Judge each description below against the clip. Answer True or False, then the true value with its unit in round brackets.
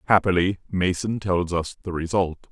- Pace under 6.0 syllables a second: True (4.7 syllables/s)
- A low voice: True (90 Hz)